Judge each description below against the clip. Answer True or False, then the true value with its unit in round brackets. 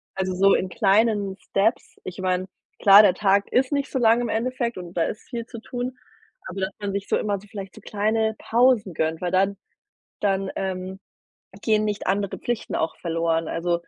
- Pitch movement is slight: False (3.1 semitones)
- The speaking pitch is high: True (200 Hz)